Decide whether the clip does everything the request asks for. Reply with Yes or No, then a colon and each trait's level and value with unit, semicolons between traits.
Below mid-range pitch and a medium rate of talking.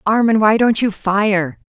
No: high, 205 Hz; average, 180 wpm